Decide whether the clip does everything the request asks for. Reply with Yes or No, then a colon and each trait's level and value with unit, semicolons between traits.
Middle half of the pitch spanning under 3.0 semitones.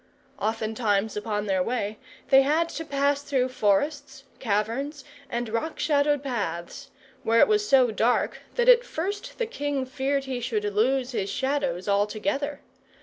No: average, 4.9 semitones